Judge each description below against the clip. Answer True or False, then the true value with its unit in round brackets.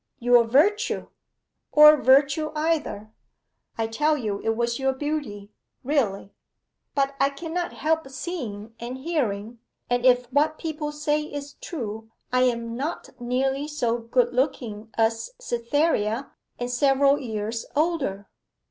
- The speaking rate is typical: False (130 wpm)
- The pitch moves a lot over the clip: False (4.6 semitones)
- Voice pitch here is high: True (260 Hz)